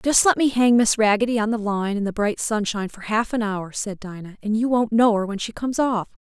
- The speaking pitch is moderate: No, high, 220 Hz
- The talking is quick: Yes, fast, 270 wpm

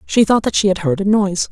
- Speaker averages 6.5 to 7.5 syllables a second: Yes, 6.6 syllables/s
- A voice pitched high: Yes, high, 195 Hz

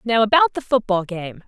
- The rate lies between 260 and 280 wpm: No, fast, 205 wpm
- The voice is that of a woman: Yes, female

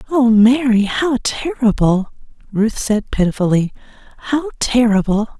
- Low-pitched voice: No, high, 235 Hz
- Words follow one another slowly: Yes, slow, 100 wpm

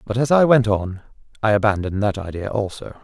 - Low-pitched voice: Yes, low, 110 Hz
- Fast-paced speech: No, average, 195 wpm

